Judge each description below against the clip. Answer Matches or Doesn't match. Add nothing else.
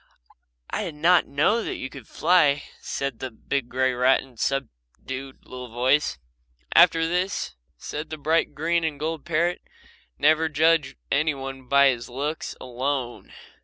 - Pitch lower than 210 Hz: Matches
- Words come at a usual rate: Matches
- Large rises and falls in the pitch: Doesn't match